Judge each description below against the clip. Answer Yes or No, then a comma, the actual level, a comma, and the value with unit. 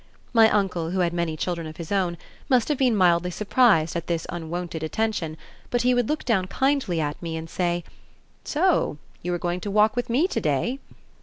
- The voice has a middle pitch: Yes, medium, 180 Hz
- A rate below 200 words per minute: No, fast, 205 wpm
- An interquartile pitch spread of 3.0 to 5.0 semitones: No, wide, 5.5 semitones